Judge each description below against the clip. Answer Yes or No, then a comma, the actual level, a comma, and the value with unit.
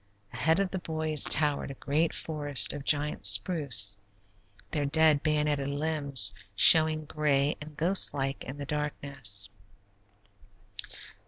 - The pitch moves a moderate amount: No, narrow, 2.1 semitones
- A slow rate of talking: Yes, slow, 120 wpm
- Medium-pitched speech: Yes, medium, 145 Hz